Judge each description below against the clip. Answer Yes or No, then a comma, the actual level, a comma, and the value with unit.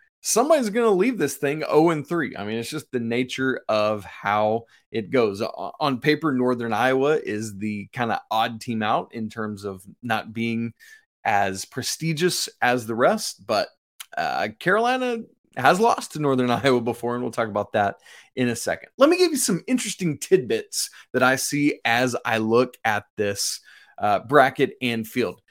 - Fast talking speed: No, average, 175 wpm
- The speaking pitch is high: No, low, 125 Hz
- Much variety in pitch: Yes, wide, 6.6 semitones